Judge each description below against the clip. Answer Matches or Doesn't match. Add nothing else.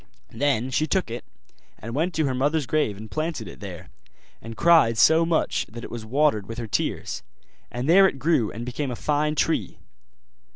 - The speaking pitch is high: Doesn't match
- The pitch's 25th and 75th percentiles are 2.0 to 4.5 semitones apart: Doesn't match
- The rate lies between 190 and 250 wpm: Matches